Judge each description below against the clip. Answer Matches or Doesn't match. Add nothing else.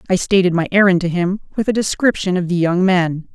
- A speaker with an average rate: Doesn't match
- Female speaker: Matches